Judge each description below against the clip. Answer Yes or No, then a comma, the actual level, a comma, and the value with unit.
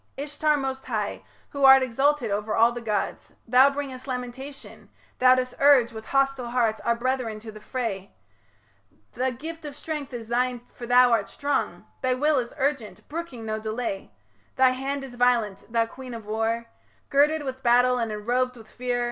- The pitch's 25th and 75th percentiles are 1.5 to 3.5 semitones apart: Yes, average, 2.8 semitones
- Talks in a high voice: Yes, very high, 250 Hz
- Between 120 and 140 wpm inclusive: No, average, 175 wpm